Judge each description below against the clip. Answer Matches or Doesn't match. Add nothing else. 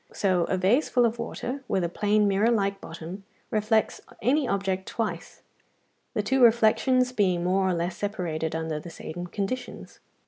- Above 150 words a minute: Matches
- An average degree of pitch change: Matches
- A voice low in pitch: Doesn't match